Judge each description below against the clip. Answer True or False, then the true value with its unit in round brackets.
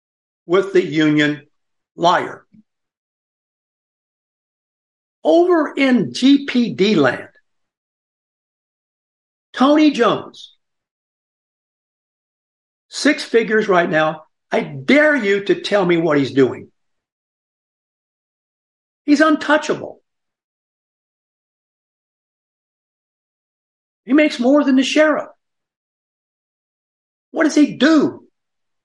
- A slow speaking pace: True (75 wpm)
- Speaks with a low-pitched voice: False (270 Hz)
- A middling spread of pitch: False (7.4 semitones)